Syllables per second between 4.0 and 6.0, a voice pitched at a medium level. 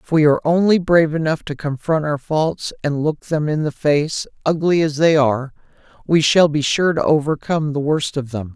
Yes: 5.2 syllables/s; medium, 150 Hz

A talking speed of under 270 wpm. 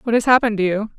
No: fast, 305 wpm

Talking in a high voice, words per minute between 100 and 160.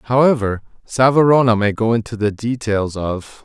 No: low, 115 Hz; average, 140 wpm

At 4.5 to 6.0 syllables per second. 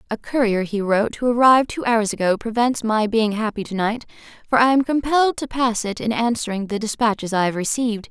Yes: 5.9 syllables/s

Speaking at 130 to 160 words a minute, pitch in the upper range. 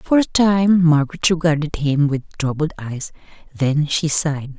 No: average, 155 wpm; medium, 155 Hz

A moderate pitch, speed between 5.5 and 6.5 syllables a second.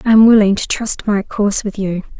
No: high, 205 Hz; 5.6 syllables/s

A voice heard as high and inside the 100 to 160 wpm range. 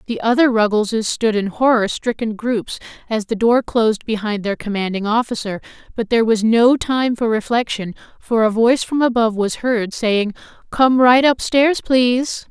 No: high, 230 Hz; average, 175 wpm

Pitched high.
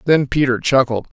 No: low, 130 Hz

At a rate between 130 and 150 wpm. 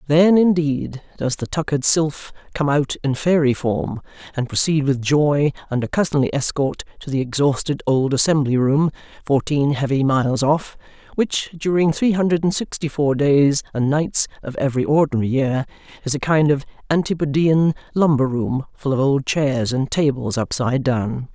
No: average, 160 wpm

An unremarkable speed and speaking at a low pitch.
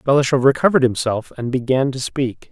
Yes: average, 165 wpm; low, 130 Hz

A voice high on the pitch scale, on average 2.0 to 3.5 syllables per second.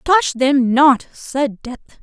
Yes: very high, 265 Hz; 3.0 syllables/s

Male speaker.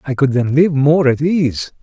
Yes: male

